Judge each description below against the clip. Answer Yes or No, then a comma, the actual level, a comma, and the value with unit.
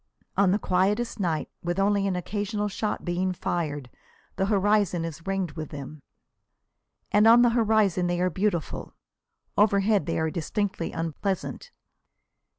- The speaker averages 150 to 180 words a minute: No, average, 140 wpm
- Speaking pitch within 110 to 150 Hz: No, high, 190 Hz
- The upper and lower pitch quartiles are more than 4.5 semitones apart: No, average, 3.3 semitones